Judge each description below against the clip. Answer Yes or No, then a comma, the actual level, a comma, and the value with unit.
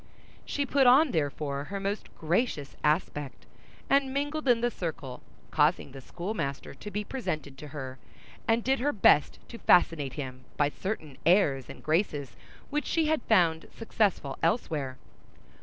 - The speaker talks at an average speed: Yes, average, 150 wpm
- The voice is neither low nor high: Yes, medium, 170 Hz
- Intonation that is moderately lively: No, wide, 8.6 semitones